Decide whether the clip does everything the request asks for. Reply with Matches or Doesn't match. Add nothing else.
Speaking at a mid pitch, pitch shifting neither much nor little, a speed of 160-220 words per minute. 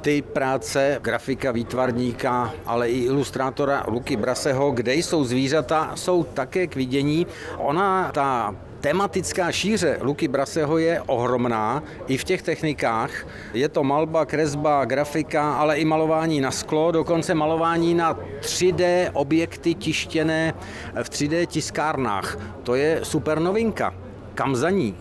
Doesn't match